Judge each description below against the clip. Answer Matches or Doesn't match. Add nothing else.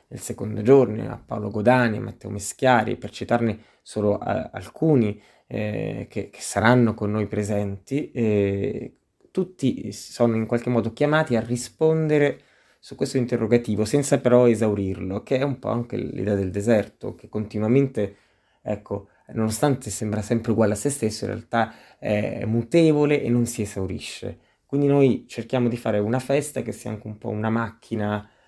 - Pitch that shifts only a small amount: Doesn't match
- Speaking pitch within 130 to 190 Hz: Doesn't match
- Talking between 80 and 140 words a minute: Doesn't match